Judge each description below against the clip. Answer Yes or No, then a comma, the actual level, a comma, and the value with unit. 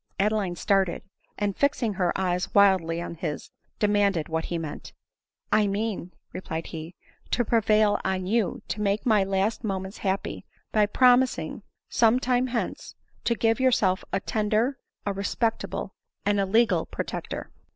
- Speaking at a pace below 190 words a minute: Yes, average, 155 wpm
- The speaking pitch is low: No, high, 205 Hz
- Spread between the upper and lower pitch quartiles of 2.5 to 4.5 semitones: Yes, average, 3.1 semitones